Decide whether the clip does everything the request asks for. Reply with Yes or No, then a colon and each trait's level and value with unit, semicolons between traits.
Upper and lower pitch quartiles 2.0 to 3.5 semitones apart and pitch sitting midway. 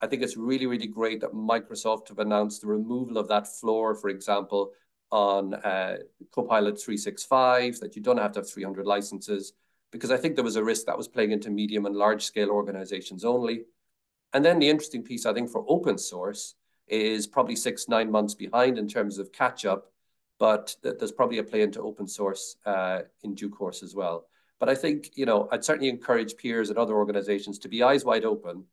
No: narrow, 2.6 semitones; low, 105 Hz